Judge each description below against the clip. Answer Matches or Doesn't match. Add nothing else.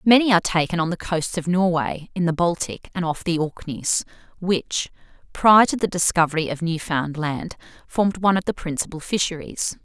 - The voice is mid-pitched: Matches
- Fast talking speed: Doesn't match